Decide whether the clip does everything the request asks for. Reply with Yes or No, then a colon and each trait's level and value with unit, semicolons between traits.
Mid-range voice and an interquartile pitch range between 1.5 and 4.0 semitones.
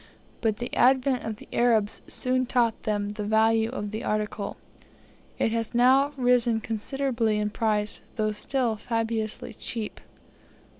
No: high, 225 Hz; narrow, 2.5 semitones